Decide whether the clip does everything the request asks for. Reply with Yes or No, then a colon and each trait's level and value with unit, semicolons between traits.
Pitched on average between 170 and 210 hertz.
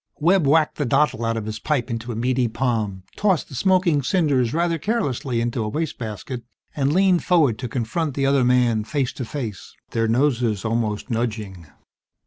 No: low, 125 Hz